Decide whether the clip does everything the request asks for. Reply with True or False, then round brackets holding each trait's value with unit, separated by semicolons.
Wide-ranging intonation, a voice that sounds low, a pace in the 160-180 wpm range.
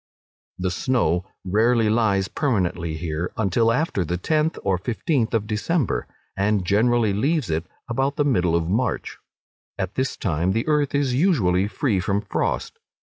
False (6.0 semitones; 105 Hz; 150 wpm)